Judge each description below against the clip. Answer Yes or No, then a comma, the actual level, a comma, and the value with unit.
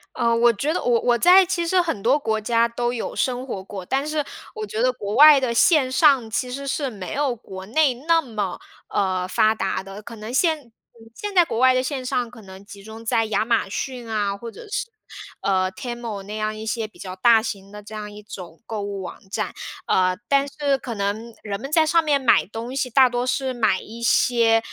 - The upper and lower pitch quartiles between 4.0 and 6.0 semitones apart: Yes, average, 4.3 semitones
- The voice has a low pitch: No, high, 235 Hz